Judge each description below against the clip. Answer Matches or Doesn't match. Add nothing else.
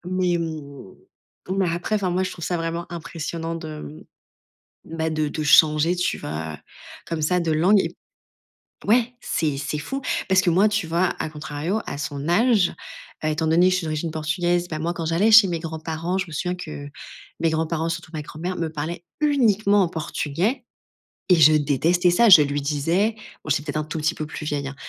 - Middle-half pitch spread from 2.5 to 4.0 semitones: Matches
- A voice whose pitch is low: Doesn't match